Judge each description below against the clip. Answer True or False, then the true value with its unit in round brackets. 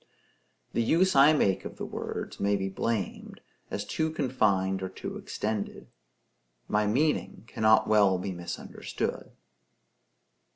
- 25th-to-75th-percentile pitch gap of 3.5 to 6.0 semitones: True (5.3 semitones)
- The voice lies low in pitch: True (105 Hz)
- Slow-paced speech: True (125 wpm)